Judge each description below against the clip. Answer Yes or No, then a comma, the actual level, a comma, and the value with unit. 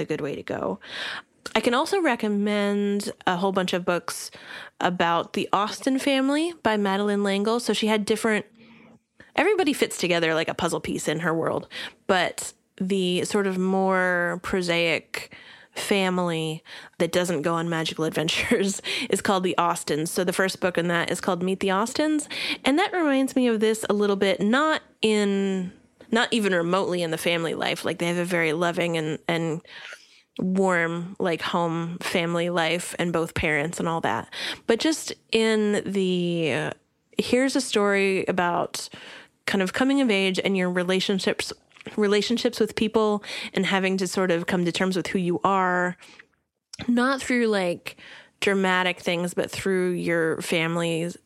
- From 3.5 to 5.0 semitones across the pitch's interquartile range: Yes, average, 4.1 semitones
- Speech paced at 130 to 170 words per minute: Yes, average, 165 wpm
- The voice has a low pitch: No, high, 190 Hz